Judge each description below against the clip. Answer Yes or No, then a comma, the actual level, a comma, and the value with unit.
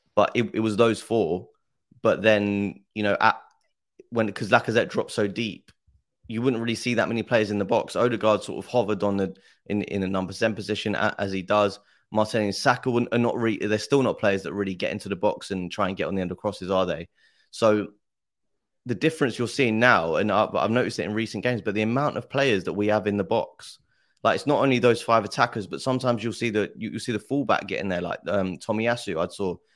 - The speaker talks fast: Yes, fast, 235 wpm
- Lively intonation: No, average, 2.7 semitones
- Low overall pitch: Yes, low, 110 Hz